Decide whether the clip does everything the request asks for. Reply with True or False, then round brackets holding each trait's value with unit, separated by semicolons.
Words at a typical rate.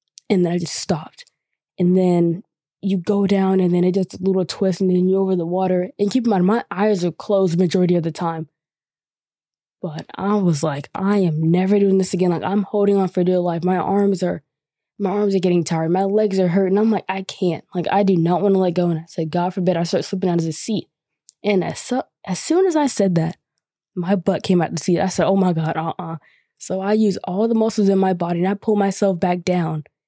False (250 wpm)